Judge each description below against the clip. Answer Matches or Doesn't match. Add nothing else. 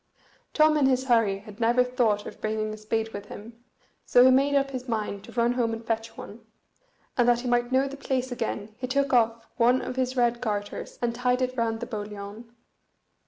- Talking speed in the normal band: Doesn't match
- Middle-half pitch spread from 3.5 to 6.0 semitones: Doesn't match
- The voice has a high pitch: Matches